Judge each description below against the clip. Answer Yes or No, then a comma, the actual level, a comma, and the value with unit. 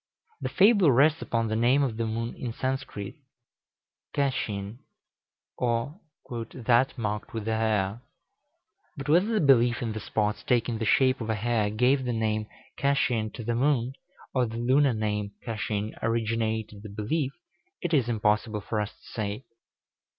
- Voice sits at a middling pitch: No, low, 115 Hz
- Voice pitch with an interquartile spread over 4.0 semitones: No, average, 3.3 semitones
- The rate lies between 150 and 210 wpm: Yes, average, 160 wpm